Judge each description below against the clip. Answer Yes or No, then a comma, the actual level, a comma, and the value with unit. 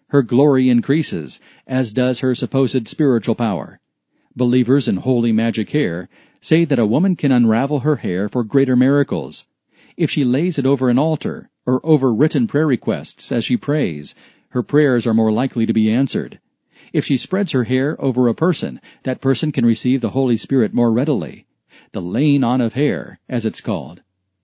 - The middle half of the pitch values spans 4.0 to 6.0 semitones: No, average, 3.2 semitones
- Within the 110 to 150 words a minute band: No, average, 180 wpm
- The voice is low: Yes, low, 130 Hz